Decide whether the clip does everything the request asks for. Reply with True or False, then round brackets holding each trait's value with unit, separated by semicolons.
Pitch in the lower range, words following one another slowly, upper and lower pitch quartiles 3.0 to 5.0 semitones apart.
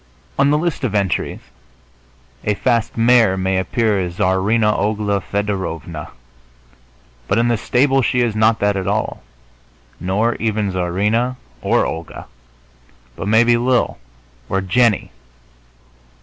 True (105 Hz; 125 wpm; 3.6 semitones)